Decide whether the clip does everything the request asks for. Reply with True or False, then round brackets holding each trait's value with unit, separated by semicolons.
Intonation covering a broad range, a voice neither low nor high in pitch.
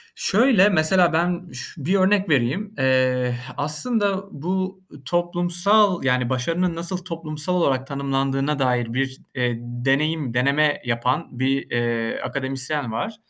True (5.7 semitones; 145 Hz)